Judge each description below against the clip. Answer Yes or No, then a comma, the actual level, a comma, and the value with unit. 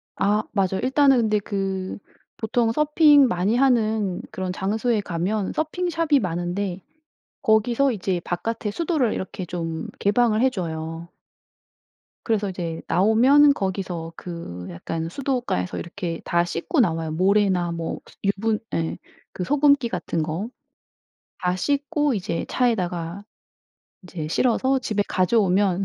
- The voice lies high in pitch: Yes, high, 200 Hz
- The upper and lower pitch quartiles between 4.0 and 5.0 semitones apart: No, wide, 5.6 semitones